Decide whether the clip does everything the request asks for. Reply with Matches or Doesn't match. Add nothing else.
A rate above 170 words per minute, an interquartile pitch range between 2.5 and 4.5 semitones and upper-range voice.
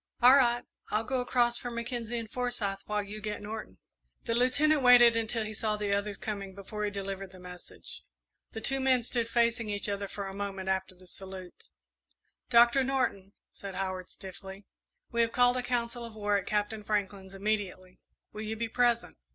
Matches